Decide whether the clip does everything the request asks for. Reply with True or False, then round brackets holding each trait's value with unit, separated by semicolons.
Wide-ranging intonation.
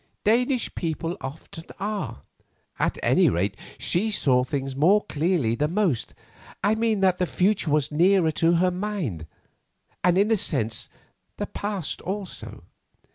True (5.8 semitones)